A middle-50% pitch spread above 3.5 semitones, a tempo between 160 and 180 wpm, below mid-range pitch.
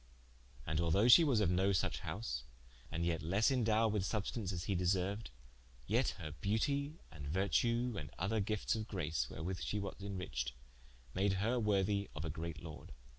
Yes: average, 4.3 semitones; average, 175 wpm; very low, 95 Hz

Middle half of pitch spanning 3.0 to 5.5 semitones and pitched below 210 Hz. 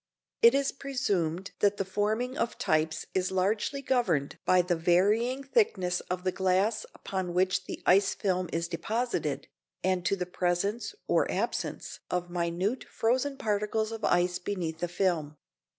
Yes: average, 4.1 semitones; high, 190 Hz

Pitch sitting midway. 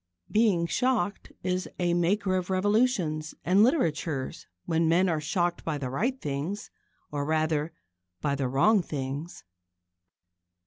Yes: medium, 170 Hz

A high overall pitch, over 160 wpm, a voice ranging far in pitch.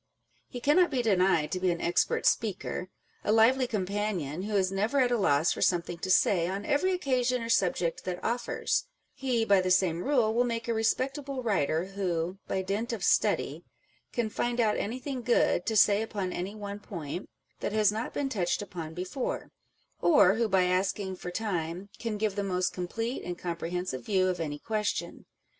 No: high, 200 Hz; average, 190 wpm; average, 4.3 semitones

